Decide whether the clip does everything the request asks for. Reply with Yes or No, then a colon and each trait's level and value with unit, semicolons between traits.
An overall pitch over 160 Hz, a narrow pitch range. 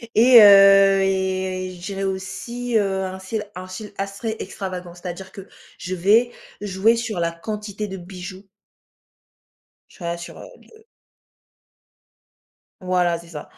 Yes: high, 190 Hz; narrow, 2.0 semitones